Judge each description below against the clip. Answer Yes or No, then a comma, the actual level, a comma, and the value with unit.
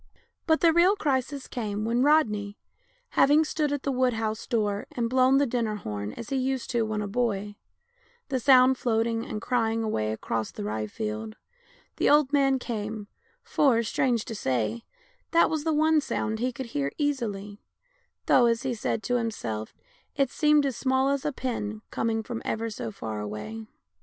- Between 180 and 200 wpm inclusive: Yes, average, 185 wpm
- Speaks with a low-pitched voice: No, high, 230 Hz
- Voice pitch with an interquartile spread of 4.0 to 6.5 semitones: Yes, average, 4.3 semitones